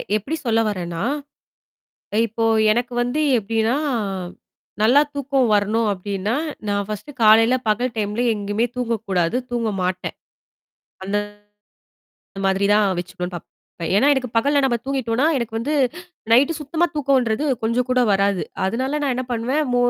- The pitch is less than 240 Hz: Yes, high, 230 Hz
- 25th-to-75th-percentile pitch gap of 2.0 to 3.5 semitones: No, average, 3.9 semitones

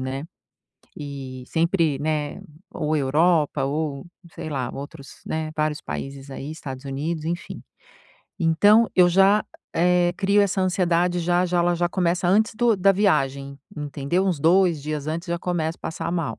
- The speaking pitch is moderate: Yes, medium, 165 Hz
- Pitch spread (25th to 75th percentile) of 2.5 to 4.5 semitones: Yes, average, 3.8 semitones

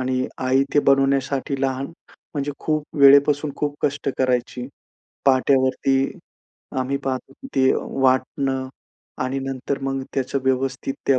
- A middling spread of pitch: No, narrow, 1.0 semitones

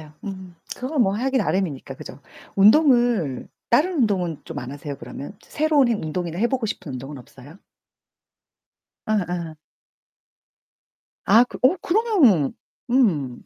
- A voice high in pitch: Yes, high, 195 Hz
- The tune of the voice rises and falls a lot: Yes, wide, 8.6 semitones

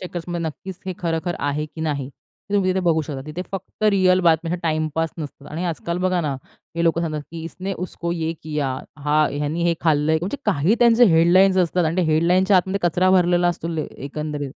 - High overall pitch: No, medium, 170 Hz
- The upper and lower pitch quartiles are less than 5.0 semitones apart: Yes, average, 2.9 semitones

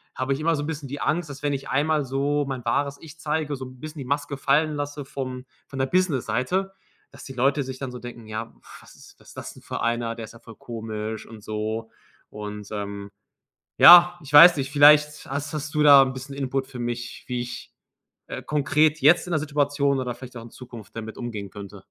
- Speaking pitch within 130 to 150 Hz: Yes, low, 135 Hz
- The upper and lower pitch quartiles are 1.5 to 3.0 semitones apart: No, average, 3.6 semitones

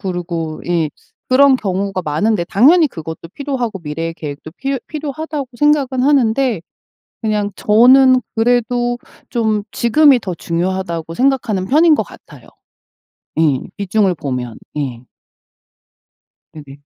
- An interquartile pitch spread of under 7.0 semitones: No, wide, 7.8 semitones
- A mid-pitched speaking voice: No, high, 215 Hz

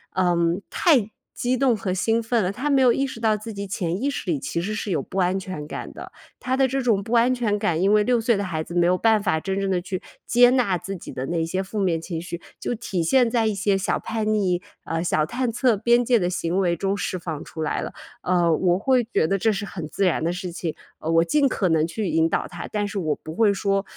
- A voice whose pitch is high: Yes, high, 195 Hz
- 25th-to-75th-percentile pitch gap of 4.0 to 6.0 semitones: Yes, average, 4.7 semitones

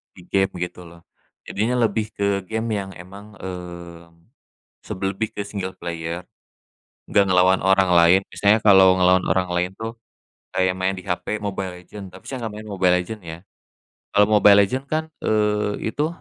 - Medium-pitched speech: No, very low, 95 Hz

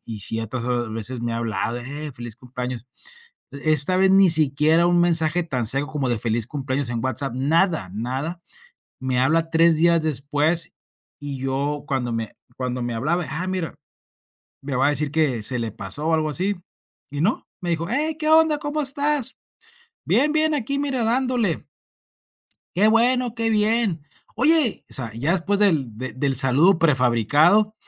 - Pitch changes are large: Yes, wide, 7.2 semitones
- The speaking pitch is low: No, medium, 155 Hz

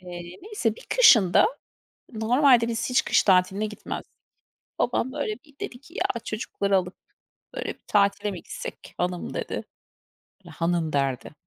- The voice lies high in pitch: Yes, high, 210 Hz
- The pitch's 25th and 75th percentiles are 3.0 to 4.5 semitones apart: No, wide, 5.5 semitones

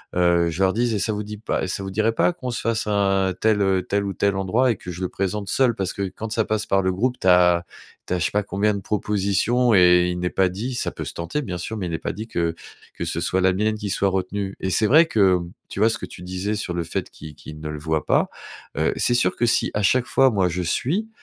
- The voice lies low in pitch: Yes, low, 100 Hz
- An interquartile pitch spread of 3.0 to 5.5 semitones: Yes, average, 3.3 semitones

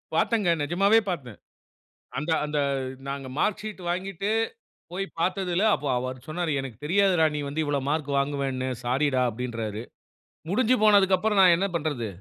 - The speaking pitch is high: No, medium, 160 Hz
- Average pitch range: No, wide, 5.8 semitones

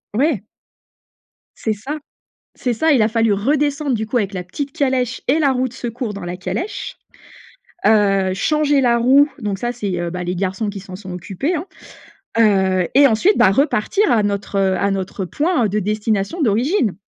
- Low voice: No, high, 220 Hz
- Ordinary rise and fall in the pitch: No, wide, 5.9 semitones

